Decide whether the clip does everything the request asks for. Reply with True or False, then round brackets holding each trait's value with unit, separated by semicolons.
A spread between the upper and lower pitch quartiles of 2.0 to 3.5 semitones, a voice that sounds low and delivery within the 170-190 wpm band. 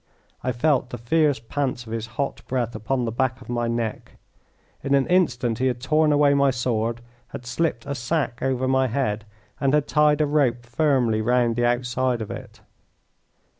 True (2.9 semitones; 125 Hz; 185 wpm)